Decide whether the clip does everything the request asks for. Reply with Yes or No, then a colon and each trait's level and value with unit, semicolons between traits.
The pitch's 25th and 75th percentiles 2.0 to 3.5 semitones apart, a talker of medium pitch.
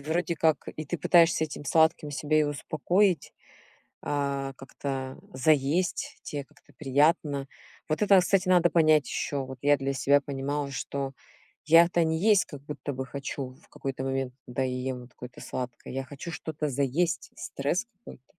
Yes: average, 3.1 semitones; medium, 145 Hz